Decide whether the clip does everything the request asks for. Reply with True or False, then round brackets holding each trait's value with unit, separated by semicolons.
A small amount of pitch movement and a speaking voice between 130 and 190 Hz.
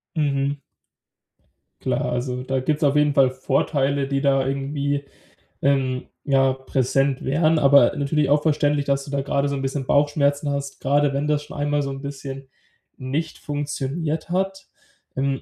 True (1.3 semitones; 140 Hz)